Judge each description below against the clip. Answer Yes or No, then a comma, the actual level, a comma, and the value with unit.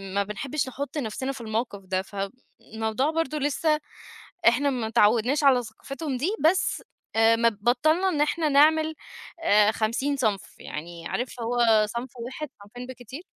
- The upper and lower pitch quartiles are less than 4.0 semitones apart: No, average, 4.6 semitones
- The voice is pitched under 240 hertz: No, very high, 250 Hz